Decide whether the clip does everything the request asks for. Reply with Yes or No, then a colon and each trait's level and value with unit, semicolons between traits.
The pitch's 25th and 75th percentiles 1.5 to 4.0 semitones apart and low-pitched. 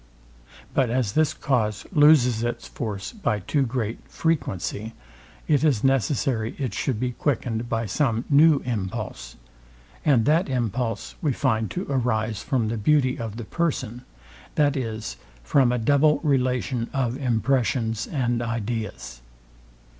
Yes: average, 3.7 semitones; low, 120 Hz